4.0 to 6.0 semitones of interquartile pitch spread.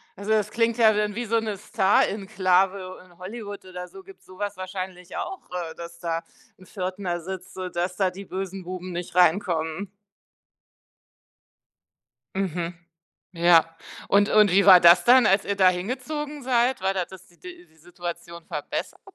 No: average, 2.8 semitones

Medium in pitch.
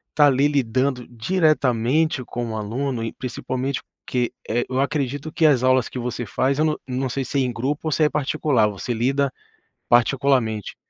No: low, 130 Hz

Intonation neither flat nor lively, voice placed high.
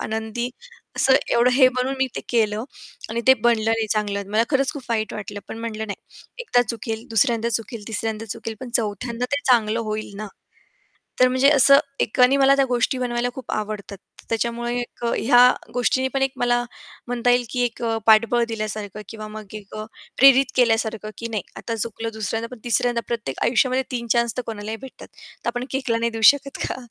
No: narrow, 2.3 semitones; high, 235 Hz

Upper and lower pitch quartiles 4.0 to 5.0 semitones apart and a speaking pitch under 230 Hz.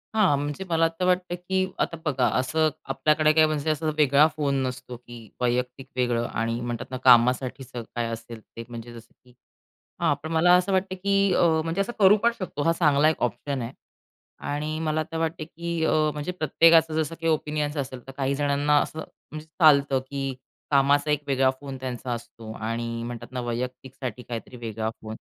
Yes: average, 4.4 semitones; medium, 140 Hz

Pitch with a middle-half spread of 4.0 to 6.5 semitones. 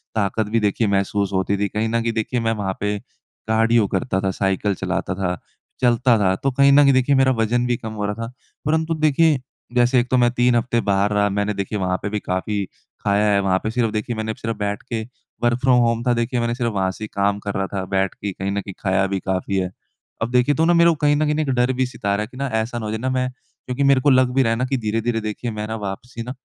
No: average, 3.6 semitones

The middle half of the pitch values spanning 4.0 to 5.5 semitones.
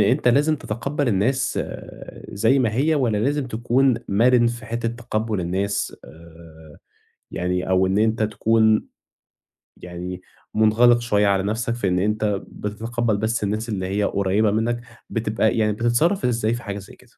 No: average, 3.0 semitones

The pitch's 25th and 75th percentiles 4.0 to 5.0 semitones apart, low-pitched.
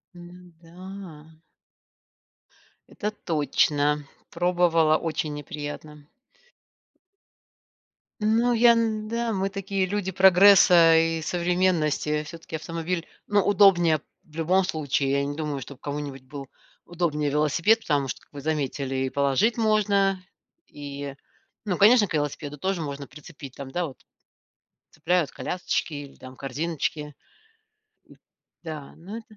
No: average, 4.5 semitones; medium, 165 Hz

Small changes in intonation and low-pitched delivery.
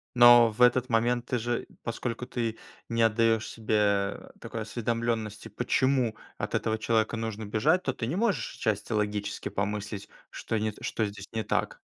Yes: narrow, 2.1 semitones; low, 115 Hz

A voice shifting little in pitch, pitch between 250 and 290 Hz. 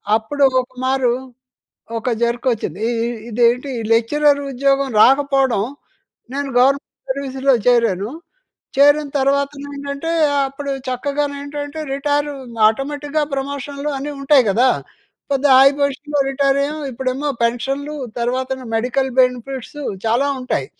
Yes: narrow, 2.2 semitones; very high, 275 Hz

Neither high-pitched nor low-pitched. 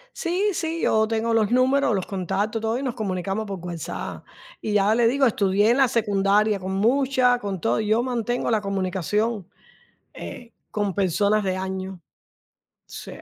No: high, 215 Hz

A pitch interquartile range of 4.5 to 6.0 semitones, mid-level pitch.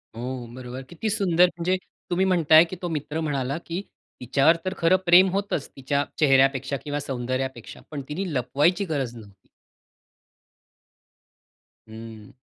Yes: average, 5.1 semitones; medium, 145 Hz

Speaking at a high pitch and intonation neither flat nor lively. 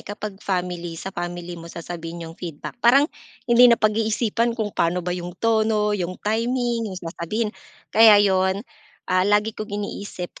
Yes: high, 205 Hz; average, 3.8 semitones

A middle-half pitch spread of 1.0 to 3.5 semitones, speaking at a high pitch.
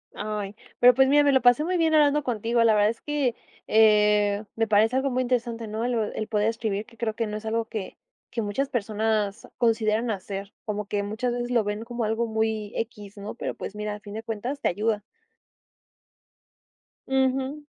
Yes: average, 2.7 semitones; high, 225 Hz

